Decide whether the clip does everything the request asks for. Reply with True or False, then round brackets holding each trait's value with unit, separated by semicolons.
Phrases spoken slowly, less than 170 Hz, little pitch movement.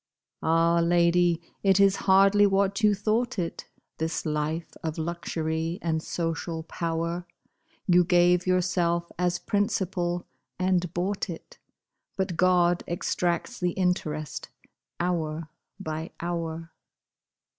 False (110 wpm; 175 Hz; 1.9 semitones)